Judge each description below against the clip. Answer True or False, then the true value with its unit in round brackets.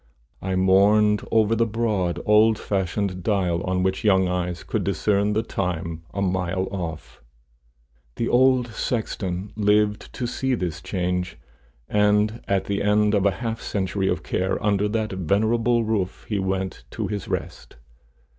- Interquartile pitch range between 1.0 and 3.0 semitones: True (2.6 semitones)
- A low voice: True (100 Hz)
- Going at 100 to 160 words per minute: True (150 wpm)